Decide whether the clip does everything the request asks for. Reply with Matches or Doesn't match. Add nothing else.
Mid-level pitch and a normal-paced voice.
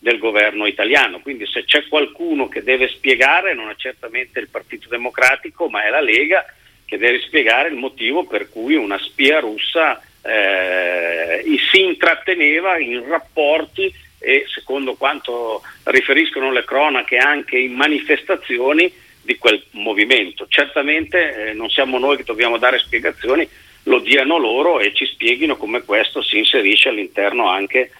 Matches